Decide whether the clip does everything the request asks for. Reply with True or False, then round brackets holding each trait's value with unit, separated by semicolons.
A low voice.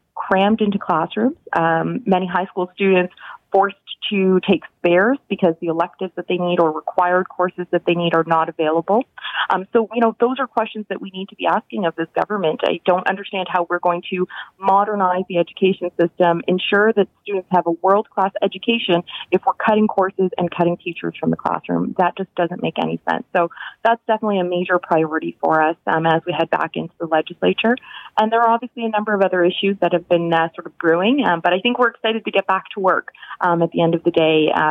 False (185 Hz)